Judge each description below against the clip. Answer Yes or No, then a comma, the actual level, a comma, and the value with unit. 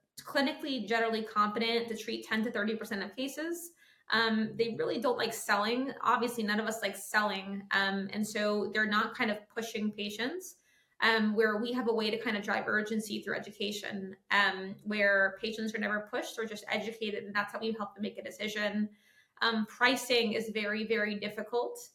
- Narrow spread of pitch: Yes, narrow, 1.7 semitones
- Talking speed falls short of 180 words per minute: No, average, 190 wpm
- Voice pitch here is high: Yes, high, 215 Hz